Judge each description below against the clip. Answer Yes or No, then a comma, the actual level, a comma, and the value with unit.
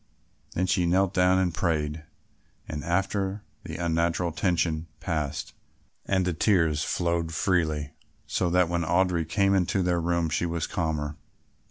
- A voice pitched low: Yes, very low, 85 Hz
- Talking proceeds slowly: No, average, 155 wpm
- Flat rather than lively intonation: Yes, narrow, 2.2 semitones